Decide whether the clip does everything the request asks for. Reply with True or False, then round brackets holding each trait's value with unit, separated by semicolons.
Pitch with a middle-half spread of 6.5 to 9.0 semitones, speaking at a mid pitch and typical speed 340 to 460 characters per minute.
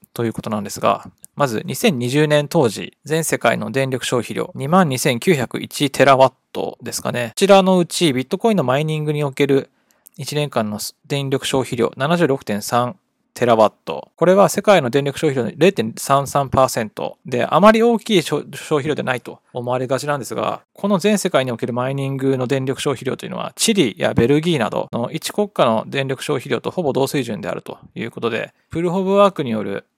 False (5.1 semitones; 145 Hz; 345 characters per minute)